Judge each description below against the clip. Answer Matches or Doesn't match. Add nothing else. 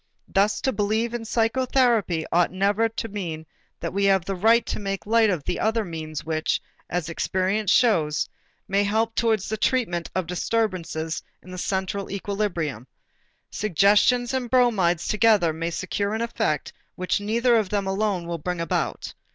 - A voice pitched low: Doesn't match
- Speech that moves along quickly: Doesn't match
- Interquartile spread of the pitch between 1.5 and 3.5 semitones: Doesn't match